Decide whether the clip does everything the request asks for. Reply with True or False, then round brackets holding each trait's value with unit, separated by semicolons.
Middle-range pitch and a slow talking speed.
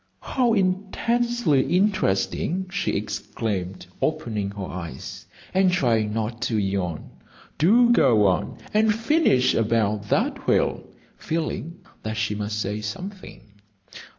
False (115 Hz; 115 wpm)